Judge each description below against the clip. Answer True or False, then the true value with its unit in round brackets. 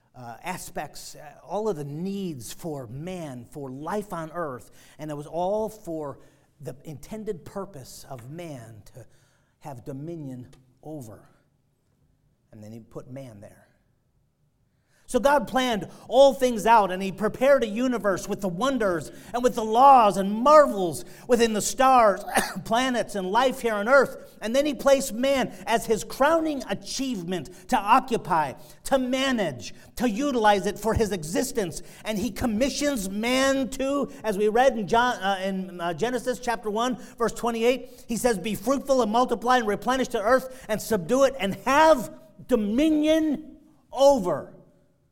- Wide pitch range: True (7.7 semitones)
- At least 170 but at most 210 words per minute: False (155 wpm)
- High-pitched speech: True (210 Hz)